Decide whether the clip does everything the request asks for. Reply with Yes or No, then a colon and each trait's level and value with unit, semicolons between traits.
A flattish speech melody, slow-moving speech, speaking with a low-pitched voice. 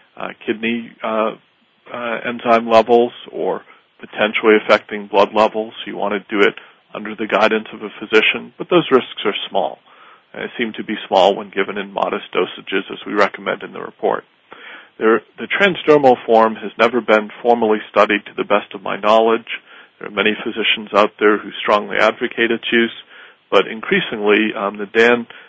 No: narrow, 1.8 semitones; average, 175 wpm; low, 110 Hz